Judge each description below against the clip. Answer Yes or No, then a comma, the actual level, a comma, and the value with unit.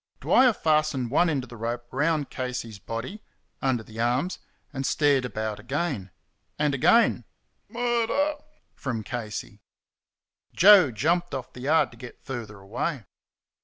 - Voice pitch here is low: Yes, low, 130 Hz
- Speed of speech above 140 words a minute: No, slow, 135 wpm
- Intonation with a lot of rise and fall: Yes, wide, 5.7 semitones